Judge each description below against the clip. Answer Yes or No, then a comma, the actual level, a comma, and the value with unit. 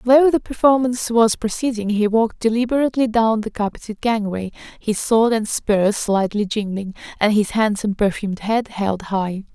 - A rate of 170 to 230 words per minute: No, average, 155 wpm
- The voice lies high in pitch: Yes, high, 220 Hz